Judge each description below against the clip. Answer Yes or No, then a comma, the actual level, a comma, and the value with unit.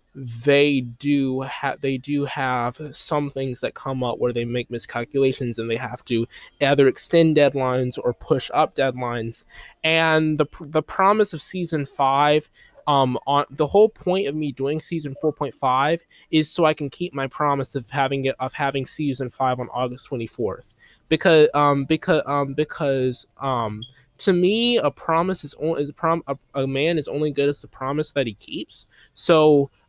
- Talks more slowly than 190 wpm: Yes, average, 180 wpm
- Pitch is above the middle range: No, medium, 140 Hz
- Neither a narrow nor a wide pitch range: Yes, average, 3.0 semitones